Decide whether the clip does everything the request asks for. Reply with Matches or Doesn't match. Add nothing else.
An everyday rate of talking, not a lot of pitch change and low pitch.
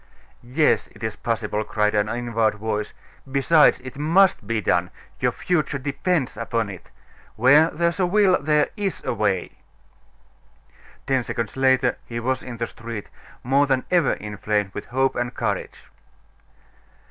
Doesn't match